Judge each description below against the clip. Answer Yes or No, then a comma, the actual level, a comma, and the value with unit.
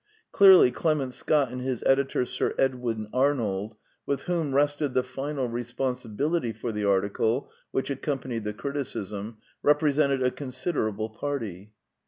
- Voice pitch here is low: Yes, low, 130 Hz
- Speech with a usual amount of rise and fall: Yes, average, 4.1 semitones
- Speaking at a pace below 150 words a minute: Yes, slow, 135 wpm